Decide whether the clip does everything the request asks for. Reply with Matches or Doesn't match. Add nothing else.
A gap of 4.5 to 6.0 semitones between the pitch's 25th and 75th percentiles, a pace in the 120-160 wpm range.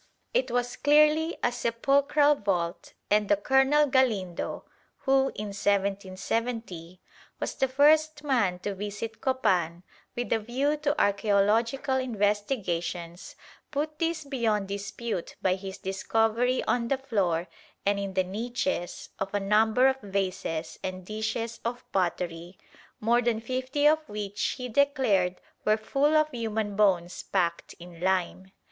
Matches